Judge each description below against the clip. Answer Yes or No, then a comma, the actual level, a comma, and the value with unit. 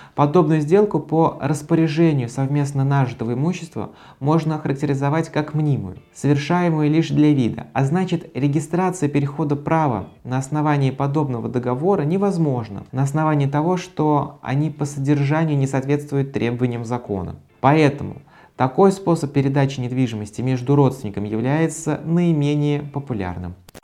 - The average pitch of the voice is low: No, medium, 145 Hz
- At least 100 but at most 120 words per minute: Yes, average, 115 wpm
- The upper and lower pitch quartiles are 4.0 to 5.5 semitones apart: No, average, 3.2 semitones